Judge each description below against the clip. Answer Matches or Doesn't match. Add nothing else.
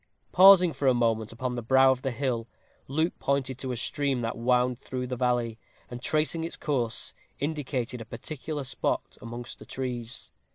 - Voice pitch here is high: Doesn't match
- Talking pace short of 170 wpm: Doesn't match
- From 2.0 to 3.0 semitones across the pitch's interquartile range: Matches